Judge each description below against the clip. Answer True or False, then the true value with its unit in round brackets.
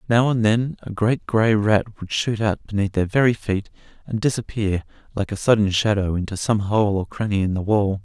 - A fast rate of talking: True (210 wpm)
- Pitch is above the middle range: False (105 Hz)